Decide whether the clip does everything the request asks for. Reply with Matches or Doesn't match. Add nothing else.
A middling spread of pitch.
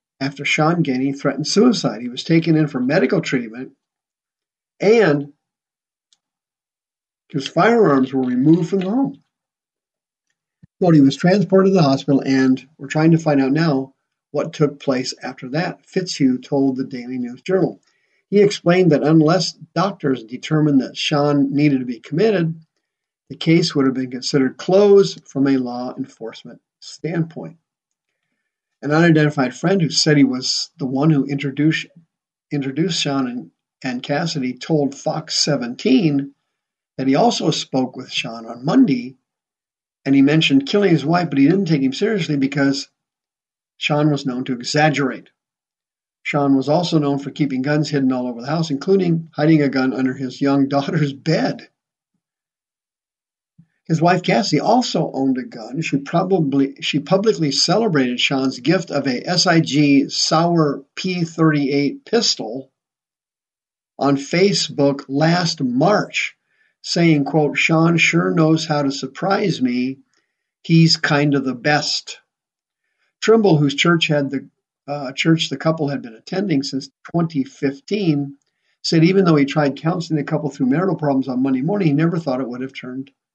Matches